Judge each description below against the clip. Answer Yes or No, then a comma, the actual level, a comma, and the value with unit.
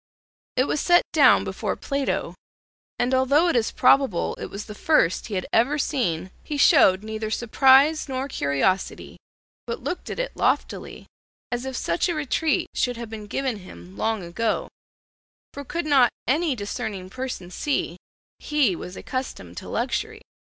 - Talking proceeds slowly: No, average, 160 wpm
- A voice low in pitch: No, very high, 250 Hz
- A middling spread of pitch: No, wide, 5.9 semitones